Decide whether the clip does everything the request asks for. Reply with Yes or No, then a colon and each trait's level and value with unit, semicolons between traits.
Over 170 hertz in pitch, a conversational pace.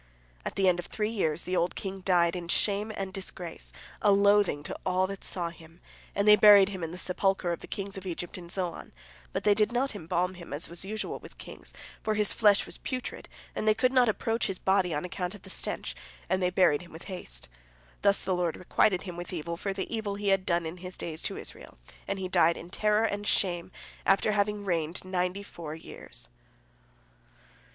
No: high, 190 Hz; fast, 215 wpm